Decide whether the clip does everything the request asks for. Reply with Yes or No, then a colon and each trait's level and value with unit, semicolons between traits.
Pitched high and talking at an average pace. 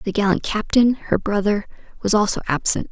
Yes: high, 205 Hz; average, 165 wpm